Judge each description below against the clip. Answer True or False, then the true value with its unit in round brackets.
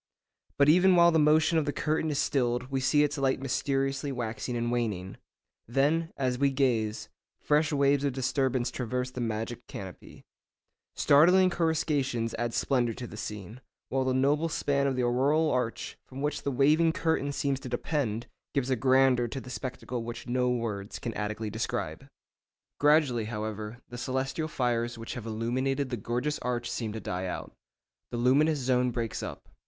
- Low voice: True (130 Hz)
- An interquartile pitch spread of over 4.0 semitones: False (3.2 semitones)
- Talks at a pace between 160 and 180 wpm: True (170 wpm)